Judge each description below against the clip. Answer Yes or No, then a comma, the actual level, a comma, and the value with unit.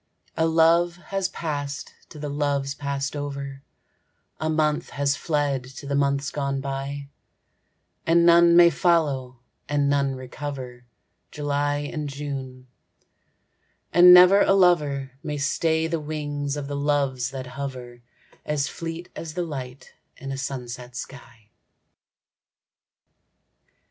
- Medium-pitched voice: Yes, medium, 145 Hz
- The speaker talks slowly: Yes, slow, 125 wpm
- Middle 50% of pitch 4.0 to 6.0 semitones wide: No, narrow, 2.6 semitones